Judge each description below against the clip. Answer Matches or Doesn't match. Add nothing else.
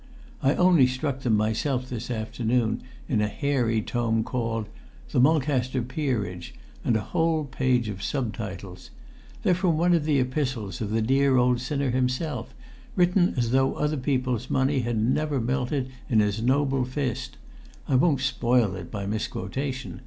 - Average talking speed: Matches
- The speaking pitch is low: Matches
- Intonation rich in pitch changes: Doesn't match